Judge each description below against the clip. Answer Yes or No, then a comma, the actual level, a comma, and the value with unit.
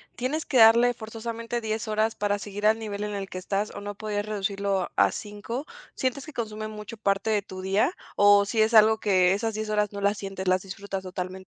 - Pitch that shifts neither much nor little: No, narrow, 1.9 semitones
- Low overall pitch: No, high, 210 Hz